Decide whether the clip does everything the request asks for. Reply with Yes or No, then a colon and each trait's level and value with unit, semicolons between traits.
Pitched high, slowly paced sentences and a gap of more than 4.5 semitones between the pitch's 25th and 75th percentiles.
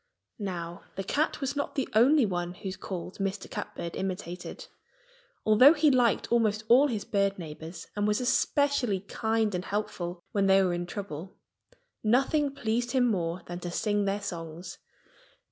No: high, 200 Hz; average, 160 wpm; average, 5.1 semitones